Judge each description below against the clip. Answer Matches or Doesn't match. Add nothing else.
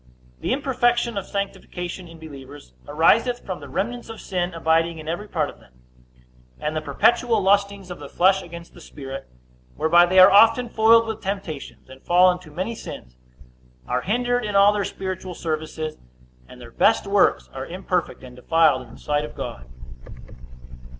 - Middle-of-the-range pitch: Matches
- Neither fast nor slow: Matches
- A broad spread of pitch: Doesn't match